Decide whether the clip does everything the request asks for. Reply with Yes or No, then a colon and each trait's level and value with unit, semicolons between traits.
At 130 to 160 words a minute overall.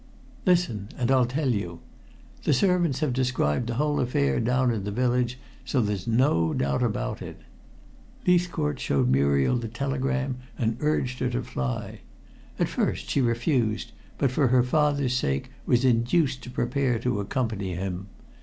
Yes: average, 155 wpm